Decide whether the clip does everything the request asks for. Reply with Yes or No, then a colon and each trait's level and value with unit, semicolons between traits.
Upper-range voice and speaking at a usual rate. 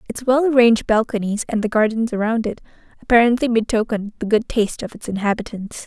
Yes: high, 225 Hz; average, 175 wpm